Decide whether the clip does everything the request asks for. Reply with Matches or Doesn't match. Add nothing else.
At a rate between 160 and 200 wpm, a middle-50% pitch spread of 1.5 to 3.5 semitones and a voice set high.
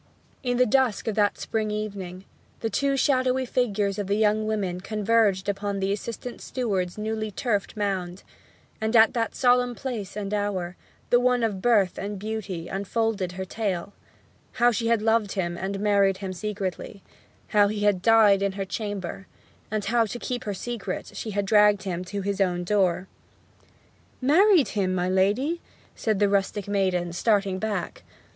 Matches